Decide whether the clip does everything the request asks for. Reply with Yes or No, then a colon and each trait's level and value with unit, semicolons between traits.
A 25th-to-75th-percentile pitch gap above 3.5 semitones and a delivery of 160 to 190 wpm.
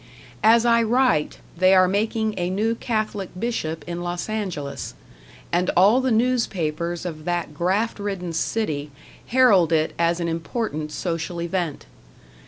No: average, 4.7 semitones; average, 140 wpm